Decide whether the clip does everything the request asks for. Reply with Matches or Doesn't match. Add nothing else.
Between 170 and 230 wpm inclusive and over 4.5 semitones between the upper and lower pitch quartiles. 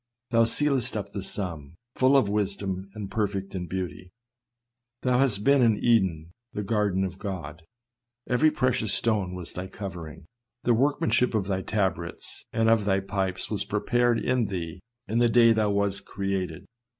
Doesn't match